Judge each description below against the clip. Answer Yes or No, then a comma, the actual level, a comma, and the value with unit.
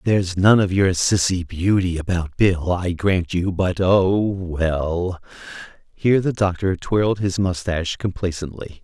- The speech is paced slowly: Yes, slow, 130 wpm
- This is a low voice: Yes, very low, 90 Hz